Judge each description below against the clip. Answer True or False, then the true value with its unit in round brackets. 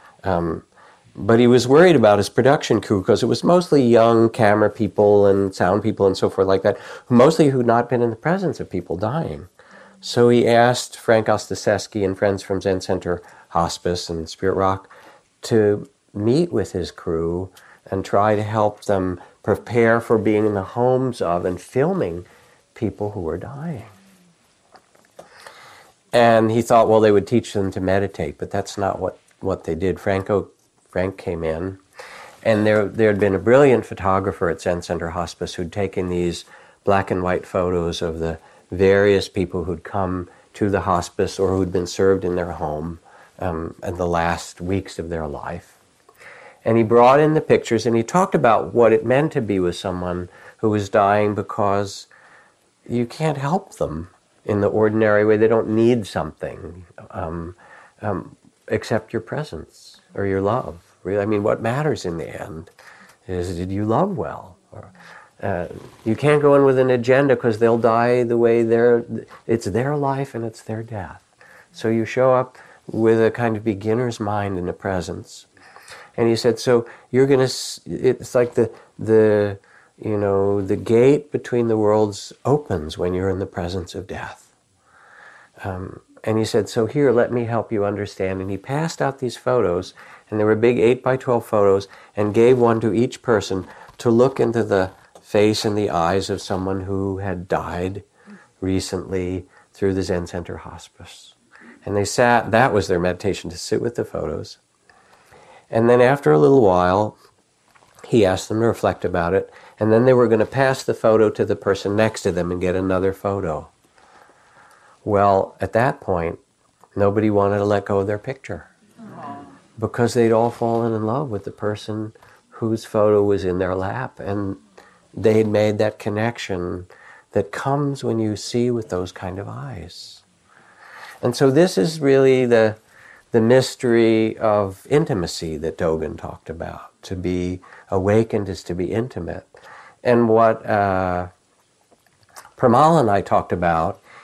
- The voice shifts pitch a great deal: False (3.6 semitones)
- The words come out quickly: False (175 wpm)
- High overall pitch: False (105 Hz)